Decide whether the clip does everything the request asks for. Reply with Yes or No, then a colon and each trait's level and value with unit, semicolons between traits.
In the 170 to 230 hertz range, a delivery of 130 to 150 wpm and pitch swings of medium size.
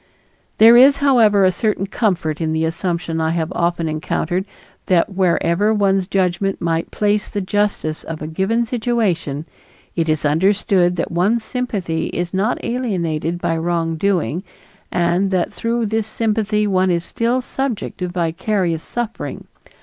Yes: medium, 185 Hz; average, 145 wpm; average, 4.1 semitones